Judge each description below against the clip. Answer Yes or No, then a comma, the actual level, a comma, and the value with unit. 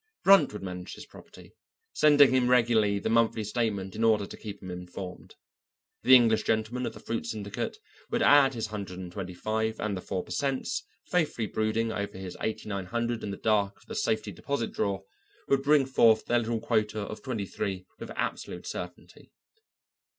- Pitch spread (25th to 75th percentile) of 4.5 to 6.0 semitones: No, average, 3.1 semitones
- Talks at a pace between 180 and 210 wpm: Yes, average, 185 wpm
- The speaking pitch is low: Yes, low, 110 Hz